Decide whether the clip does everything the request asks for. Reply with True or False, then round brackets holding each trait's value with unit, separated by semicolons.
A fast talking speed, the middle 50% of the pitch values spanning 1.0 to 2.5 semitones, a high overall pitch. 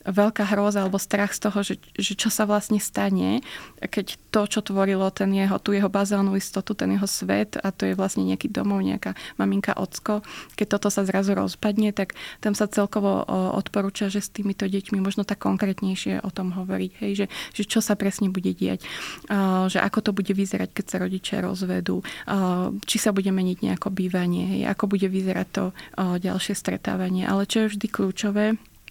True (185 wpm; 1.8 semitones; 195 Hz)